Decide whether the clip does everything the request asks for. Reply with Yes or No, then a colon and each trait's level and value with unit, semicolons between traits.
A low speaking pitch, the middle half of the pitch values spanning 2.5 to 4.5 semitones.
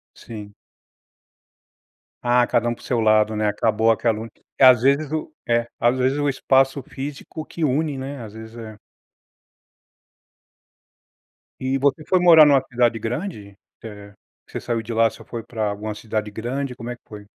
Yes: low, 120 Hz; average, 3.6 semitones